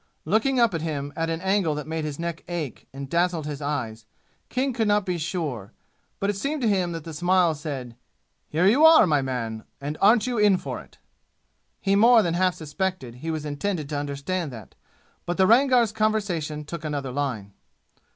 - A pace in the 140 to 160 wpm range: No, average, 195 wpm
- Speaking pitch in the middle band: Yes, medium, 165 Hz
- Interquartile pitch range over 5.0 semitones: Yes, wide, 5.6 semitones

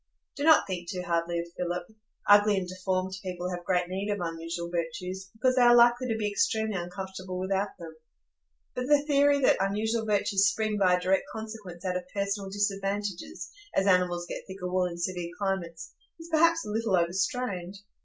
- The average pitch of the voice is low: No, high, 190 Hz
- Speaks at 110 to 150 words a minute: No, average, 185 wpm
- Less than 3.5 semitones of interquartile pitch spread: Yes, average, 3.0 semitones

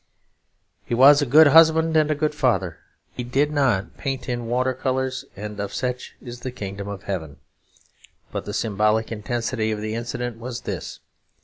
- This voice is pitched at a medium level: No, low, 120 Hz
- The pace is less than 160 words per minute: No, average, 175 wpm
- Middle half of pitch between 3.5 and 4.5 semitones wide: Yes, average, 4.0 semitones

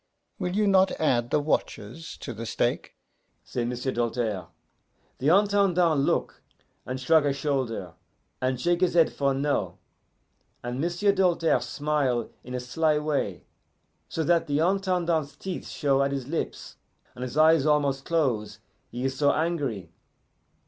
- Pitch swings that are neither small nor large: Yes, average, 4.9 semitones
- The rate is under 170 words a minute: Yes, average, 150 wpm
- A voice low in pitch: No, medium, 145 Hz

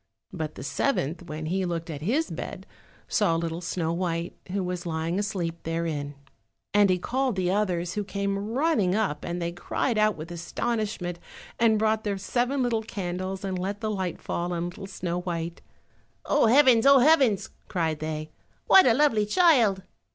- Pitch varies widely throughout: No, average, 4.3 semitones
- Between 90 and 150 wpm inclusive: No, average, 175 wpm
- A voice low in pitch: No, high, 190 Hz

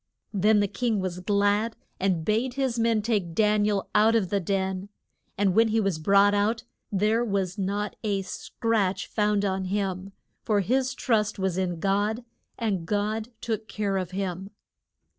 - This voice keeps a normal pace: Yes, average, 170 wpm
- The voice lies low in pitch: No, high, 205 Hz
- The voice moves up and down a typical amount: No, narrow, 2.3 semitones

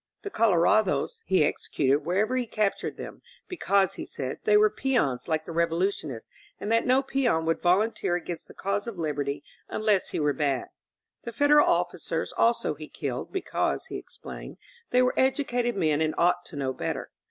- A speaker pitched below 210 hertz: Yes, high, 190 Hz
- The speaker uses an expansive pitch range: Yes, wide, 7.0 semitones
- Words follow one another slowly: No, average, 185 wpm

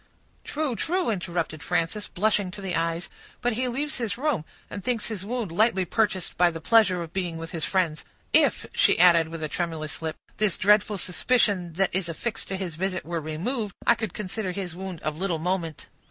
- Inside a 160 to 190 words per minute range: No, average, 200 wpm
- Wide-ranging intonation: No, average, 4.4 semitones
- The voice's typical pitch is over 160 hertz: Yes, medium, 185 Hz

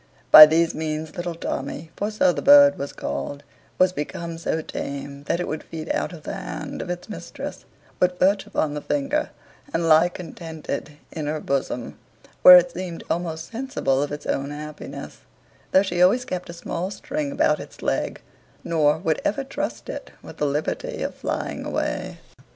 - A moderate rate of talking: Yes, average, 180 wpm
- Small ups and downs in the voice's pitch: No, average, 3.6 semitones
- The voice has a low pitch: No, medium, 170 Hz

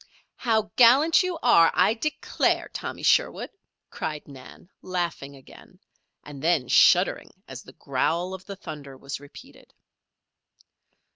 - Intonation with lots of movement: Yes, wide, 7.5 semitones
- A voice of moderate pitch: Yes, medium, 175 Hz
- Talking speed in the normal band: No, slow, 125 wpm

